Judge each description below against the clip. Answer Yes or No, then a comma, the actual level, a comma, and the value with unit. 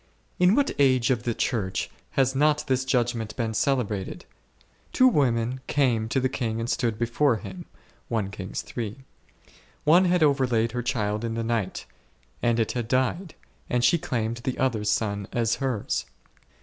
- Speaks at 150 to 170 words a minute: Yes, average, 160 wpm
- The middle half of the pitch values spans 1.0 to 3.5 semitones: Yes, average, 3.1 semitones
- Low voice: Yes, low, 120 Hz